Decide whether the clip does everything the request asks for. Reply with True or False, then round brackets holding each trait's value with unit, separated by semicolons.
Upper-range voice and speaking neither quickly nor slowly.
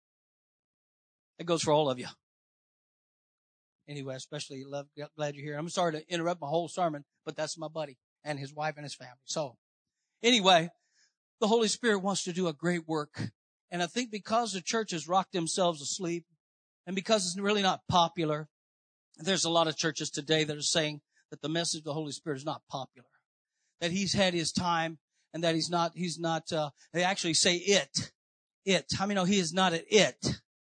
False (165 Hz; 195 wpm)